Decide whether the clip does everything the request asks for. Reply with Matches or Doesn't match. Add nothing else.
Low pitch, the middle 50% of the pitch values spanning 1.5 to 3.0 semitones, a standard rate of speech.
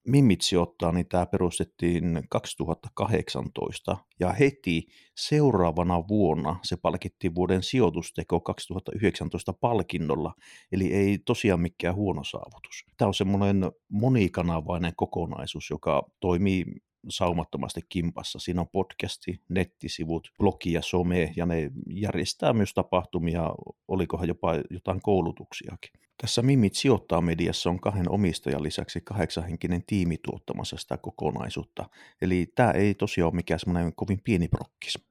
Matches